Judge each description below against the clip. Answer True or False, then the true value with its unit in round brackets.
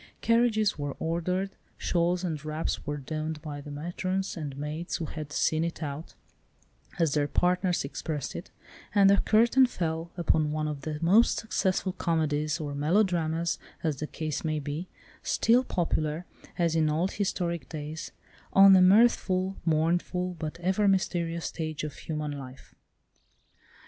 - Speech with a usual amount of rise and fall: True (3.3 semitones)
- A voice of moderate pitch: True (165 Hz)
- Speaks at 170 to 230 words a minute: False (150 wpm)